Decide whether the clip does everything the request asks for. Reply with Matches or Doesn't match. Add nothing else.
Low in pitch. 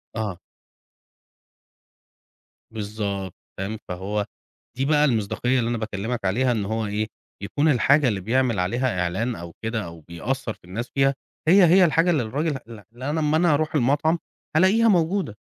Matches